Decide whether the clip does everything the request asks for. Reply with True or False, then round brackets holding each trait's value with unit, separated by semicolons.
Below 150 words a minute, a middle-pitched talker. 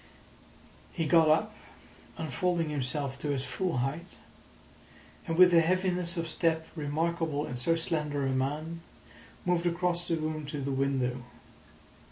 True (140 wpm; 160 Hz)